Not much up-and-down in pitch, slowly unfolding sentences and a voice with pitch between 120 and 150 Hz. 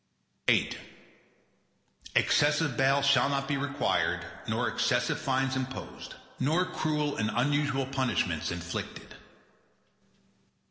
Yes: narrow, 1.9 semitones; slow, 95 wpm; low, 135 Hz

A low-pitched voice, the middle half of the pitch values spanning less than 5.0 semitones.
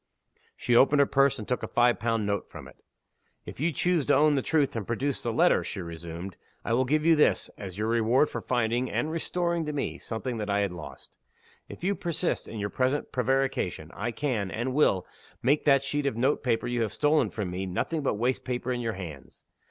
No: low, 125 Hz; average, 5.3 semitones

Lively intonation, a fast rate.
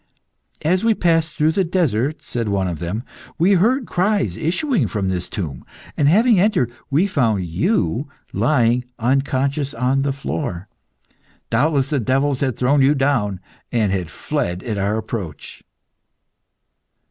No: wide, 7.1 semitones; average, 145 wpm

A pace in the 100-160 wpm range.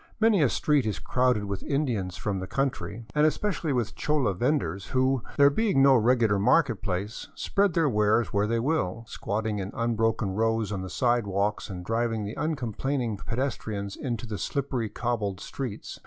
No: average, 170 wpm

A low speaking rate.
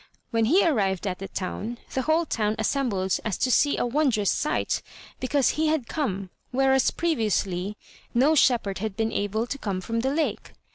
No: average, 180 wpm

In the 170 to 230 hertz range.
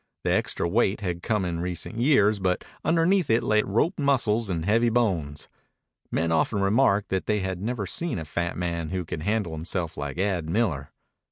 No: very low, 95 Hz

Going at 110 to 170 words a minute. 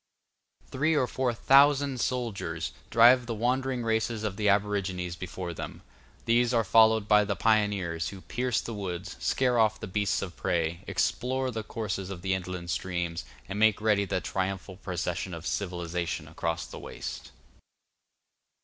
Yes: average, 155 wpm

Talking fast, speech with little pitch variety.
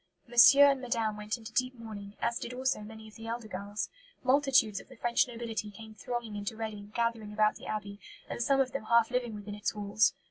Yes: fast, 215 wpm; narrow, 2.3 semitones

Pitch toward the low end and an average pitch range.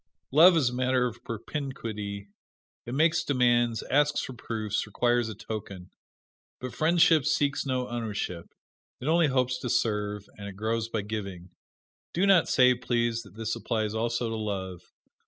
Yes: low, 120 Hz; average, 3.5 semitones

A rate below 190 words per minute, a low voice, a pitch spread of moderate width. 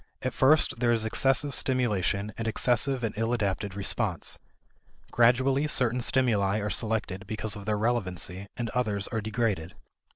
Yes: average, 150 wpm; low, 110 Hz; average, 3.5 semitones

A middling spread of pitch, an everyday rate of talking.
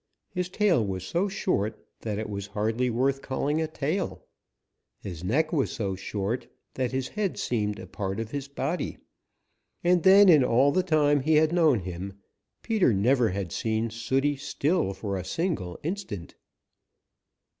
No: wide, 7.6 semitones; average, 160 wpm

